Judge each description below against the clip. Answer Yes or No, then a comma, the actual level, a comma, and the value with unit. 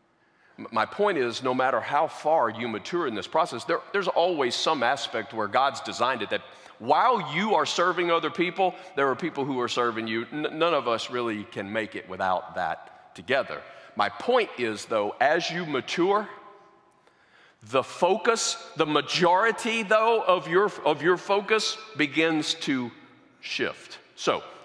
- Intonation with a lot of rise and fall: Yes, wide, 6.6 semitones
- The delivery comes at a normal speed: Yes, average, 165 wpm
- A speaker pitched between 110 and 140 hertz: No, medium, 170 Hz